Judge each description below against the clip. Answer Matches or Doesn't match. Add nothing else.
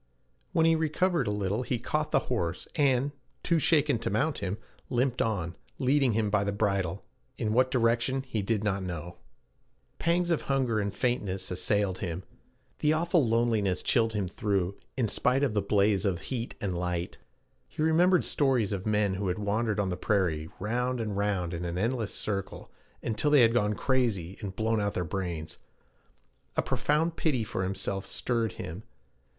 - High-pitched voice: Doesn't match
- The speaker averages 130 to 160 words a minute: Doesn't match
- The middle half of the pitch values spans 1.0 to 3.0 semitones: Doesn't match